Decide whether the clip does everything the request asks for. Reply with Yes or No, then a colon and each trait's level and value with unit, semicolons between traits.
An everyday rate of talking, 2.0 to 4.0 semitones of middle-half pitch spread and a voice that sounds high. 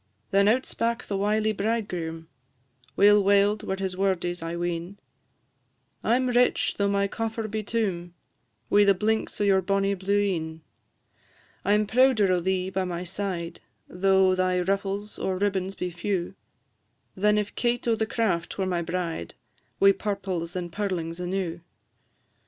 Yes: average, 155 wpm; narrow, 2.6 semitones; high, 195 Hz